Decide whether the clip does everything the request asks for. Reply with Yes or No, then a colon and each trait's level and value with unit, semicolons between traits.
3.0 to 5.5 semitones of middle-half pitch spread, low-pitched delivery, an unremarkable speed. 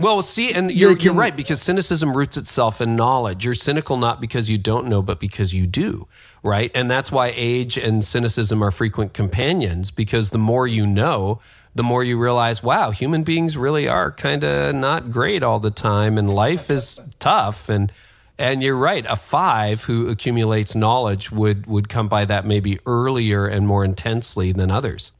Yes: average, 3.8 semitones; low, 115 Hz; average, 190 wpm